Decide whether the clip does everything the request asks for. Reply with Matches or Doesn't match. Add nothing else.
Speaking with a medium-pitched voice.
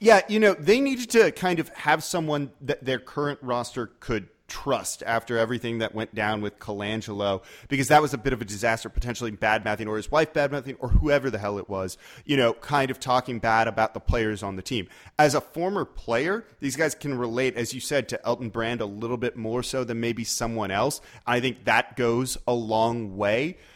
Doesn't match